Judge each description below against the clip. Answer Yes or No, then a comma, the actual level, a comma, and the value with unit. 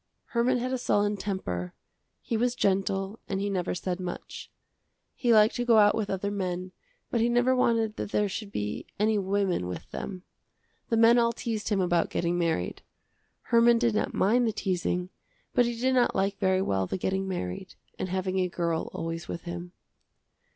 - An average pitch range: Yes, average, 4.2 semitones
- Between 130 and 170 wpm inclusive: No, average, 185 wpm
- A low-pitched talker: No, high, 195 Hz